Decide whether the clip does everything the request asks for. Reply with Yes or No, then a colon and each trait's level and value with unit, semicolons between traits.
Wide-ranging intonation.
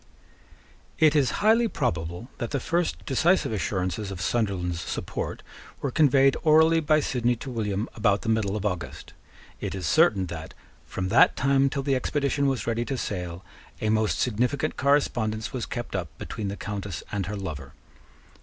Yes: wide, 6.0 semitones